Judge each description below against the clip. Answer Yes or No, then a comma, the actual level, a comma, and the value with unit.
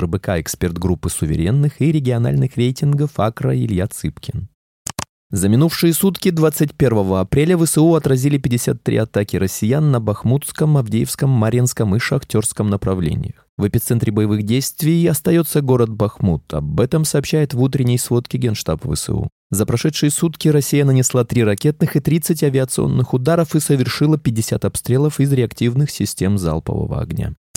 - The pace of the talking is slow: No, average, 135 wpm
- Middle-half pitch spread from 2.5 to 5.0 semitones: No, wide, 5.5 semitones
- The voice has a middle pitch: No, low, 130 Hz